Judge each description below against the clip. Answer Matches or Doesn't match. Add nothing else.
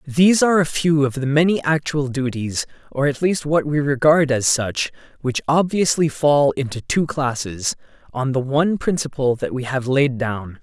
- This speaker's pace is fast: Doesn't match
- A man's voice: Matches